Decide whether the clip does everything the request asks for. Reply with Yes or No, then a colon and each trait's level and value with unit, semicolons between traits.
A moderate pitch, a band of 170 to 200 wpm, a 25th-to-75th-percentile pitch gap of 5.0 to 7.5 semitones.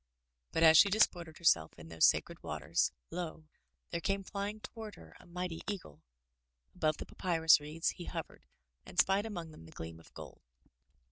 No: medium, 165 Hz; average, 175 wpm; average, 4.3 semitones